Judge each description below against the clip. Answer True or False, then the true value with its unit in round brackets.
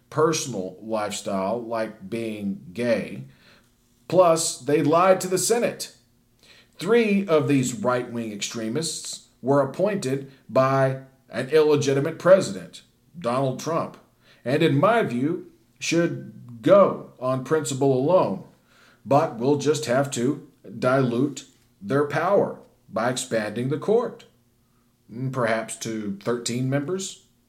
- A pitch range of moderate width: True (4.9 semitones)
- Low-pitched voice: True (130 Hz)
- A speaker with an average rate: False (110 wpm)